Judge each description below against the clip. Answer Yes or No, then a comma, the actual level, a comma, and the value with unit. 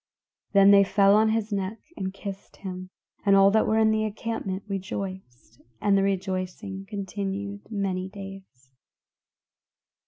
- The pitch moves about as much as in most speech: No, narrow, 1.3 semitones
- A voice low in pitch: No, high, 195 Hz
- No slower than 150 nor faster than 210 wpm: No, slow, 135 wpm